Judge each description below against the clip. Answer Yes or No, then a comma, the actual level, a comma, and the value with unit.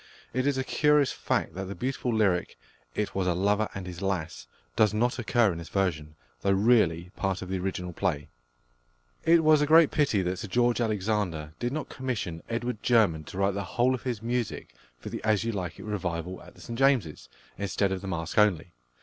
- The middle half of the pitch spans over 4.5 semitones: Yes, average, 5.2 semitones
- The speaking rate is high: Yes, fast, 210 wpm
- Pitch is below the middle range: Yes, low, 100 Hz